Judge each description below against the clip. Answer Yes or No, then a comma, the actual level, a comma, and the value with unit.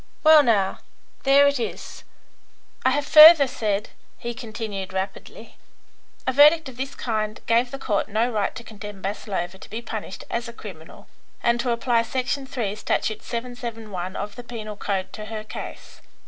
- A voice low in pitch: No, high, 230 Hz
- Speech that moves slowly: No, average, 165 wpm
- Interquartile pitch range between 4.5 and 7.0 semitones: No, average, 3.5 semitones